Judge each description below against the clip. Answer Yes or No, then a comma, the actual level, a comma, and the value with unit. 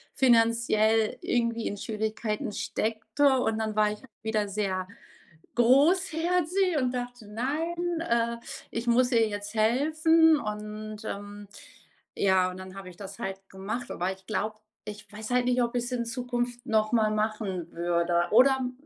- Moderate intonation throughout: Yes, average, 3.1 semitones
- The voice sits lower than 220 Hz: No, high, 225 Hz